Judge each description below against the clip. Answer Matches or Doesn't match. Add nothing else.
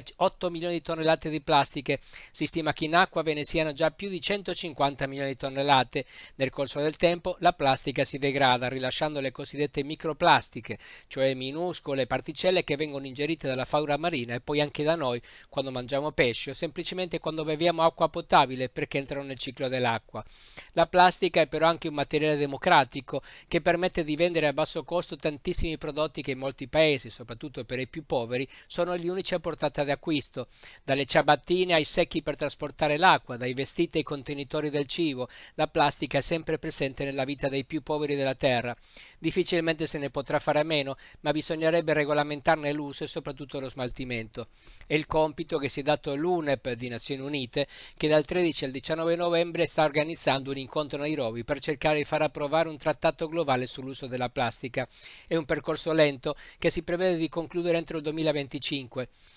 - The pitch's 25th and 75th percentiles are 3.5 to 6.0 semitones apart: Doesn't match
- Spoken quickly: Matches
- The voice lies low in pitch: Doesn't match